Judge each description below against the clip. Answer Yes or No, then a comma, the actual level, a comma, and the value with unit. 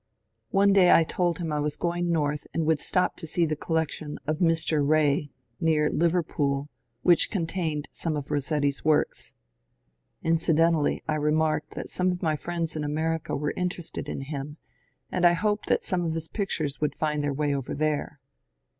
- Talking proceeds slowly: No, average, 180 wpm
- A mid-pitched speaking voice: Yes, medium, 155 Hz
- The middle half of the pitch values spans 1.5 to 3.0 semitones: Yes, narrow, 2.4 semitones